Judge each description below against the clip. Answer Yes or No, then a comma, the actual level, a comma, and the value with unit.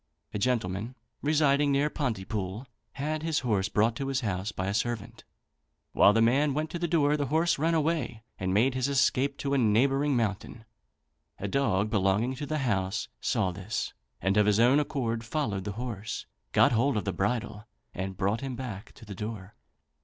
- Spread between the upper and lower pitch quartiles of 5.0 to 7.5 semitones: Yes, wide, 5.4 semitones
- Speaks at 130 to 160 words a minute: No, average, 185 wpm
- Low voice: Yes, low, 115 Hz